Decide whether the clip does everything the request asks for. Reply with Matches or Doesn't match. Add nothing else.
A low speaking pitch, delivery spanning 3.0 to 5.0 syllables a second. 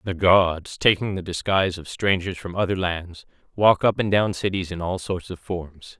Matches